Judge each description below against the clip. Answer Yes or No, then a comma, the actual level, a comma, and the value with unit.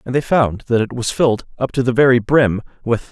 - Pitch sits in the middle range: No, low, 120 Hz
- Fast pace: Yes, fast, 250 wpm